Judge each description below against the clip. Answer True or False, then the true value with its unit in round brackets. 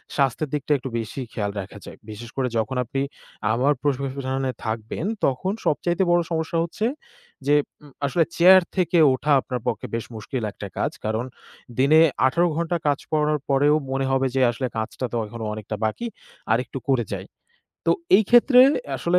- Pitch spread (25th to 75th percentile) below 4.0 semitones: False (5.0 semitones)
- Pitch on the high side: False (135 Hz)